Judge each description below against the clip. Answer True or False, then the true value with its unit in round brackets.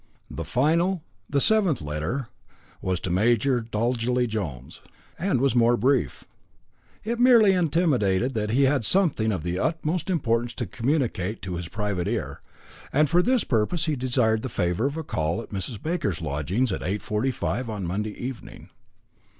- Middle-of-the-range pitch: False (120 Hz)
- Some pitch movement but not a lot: False (6.7 semitones)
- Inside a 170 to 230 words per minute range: False (160 wpm)